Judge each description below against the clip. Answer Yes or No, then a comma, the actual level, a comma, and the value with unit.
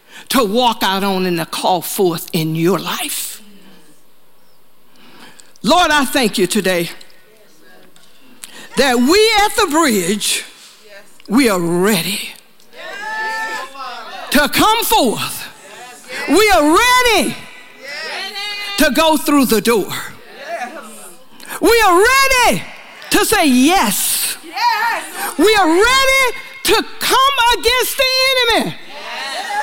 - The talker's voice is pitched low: No, very high, 305 Hz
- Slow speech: Yes, slow, 100 wpm